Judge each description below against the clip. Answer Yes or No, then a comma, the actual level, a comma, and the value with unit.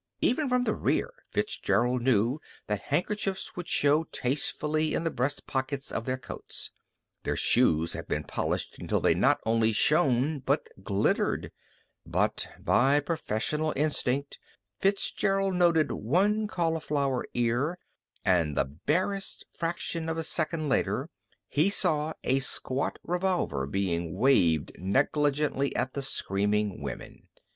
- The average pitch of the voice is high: No, medium, 140 Hz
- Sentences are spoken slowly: Yes, slow, 130 wpm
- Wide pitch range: Yes, wide, 6.1 semitones